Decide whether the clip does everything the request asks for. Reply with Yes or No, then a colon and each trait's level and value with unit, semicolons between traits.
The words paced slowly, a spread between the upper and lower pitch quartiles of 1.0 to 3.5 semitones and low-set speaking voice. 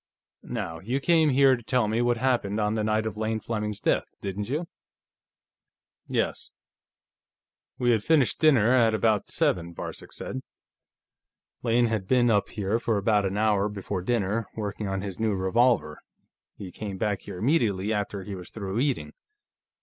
No: average, 165 wpm; average, 3.2 semitones; low, 110 Hz